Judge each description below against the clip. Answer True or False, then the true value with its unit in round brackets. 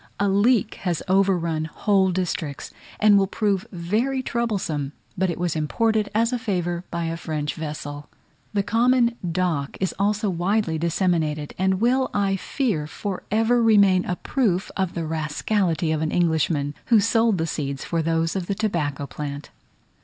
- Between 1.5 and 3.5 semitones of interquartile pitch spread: False (4.7 semitones)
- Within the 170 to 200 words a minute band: False (160 wpm)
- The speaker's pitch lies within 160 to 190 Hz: True (185 Hz)